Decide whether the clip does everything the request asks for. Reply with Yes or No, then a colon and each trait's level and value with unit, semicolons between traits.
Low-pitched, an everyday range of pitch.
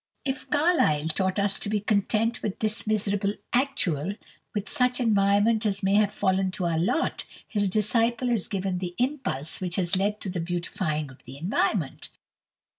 No: high, 200 Hz; average, 3.6 semitones